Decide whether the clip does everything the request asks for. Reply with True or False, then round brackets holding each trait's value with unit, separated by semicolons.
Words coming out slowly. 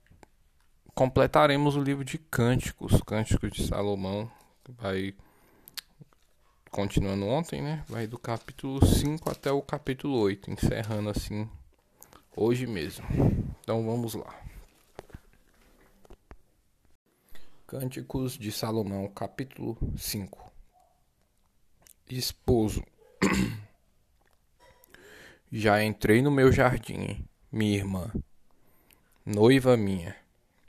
True (85 wpm)